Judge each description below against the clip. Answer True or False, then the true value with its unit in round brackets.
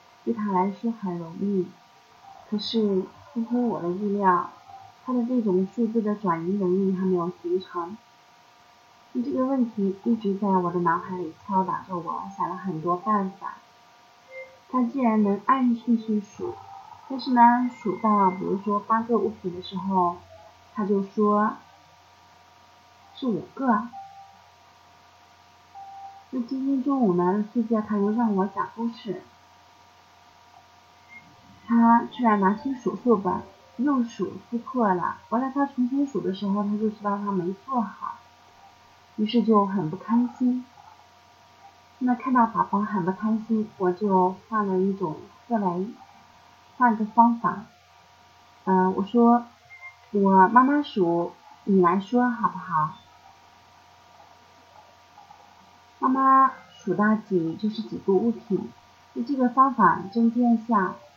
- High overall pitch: True (215 Hz)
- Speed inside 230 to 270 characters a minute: False (185 characters per minute)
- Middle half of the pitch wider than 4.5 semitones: False (4.2 semitones)